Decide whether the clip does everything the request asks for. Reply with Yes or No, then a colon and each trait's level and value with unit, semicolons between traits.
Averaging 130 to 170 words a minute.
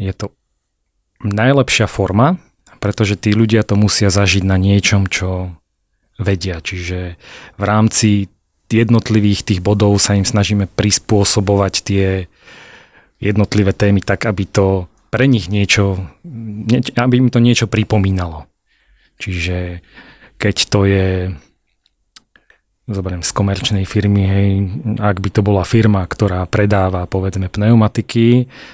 No: average, 120 wpm